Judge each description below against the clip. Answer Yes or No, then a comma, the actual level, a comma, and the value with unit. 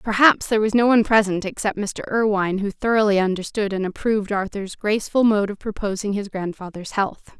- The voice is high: Yes, high, 205 Hz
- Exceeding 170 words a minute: Yes, average, 180 wpm